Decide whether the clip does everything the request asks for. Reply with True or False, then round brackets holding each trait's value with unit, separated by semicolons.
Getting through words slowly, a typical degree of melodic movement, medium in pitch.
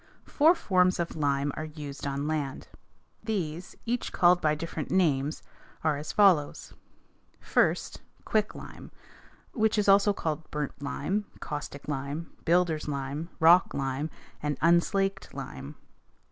True (125 wpm; 4.3 semitones; 160 Hz)